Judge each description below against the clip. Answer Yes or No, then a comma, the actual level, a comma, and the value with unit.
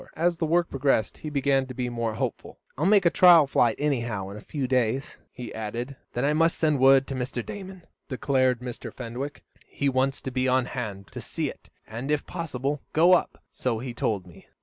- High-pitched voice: No, low, 130 Hz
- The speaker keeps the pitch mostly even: No, average, 3.6 semitones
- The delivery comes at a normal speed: No, fast, 210 wpm